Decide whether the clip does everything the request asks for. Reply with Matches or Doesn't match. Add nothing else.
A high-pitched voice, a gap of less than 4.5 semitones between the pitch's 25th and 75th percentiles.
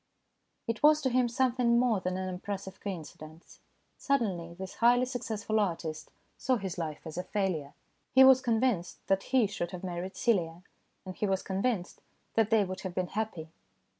Doesn't match